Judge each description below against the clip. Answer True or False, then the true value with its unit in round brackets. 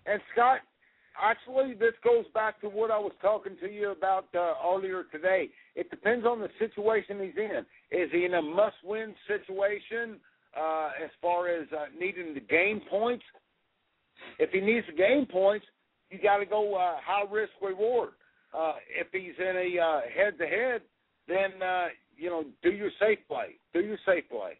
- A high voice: True (205 Hz)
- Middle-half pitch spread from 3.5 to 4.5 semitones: True (3.9 semitones)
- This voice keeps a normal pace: True (180 wpm)